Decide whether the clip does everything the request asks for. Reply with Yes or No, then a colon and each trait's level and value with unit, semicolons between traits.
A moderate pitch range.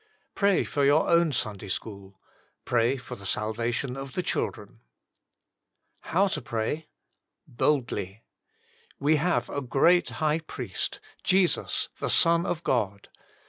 No: wide, 6.7 semitones